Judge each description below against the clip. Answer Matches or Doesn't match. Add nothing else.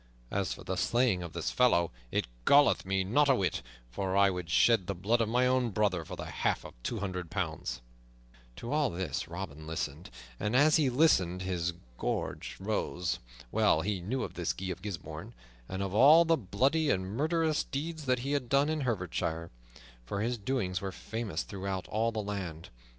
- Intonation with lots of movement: Matches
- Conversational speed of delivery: Matches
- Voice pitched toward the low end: Matches